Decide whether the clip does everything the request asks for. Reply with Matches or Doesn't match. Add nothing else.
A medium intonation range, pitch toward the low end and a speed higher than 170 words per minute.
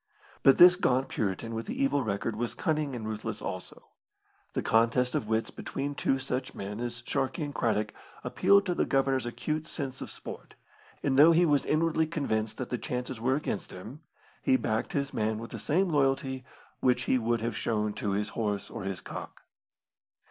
Matches